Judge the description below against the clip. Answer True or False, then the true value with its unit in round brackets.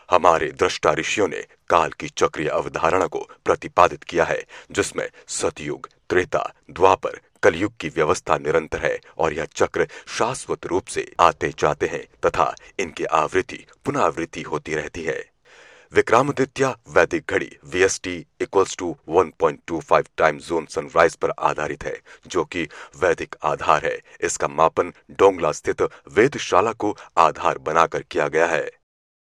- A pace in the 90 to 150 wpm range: True (145 wpm)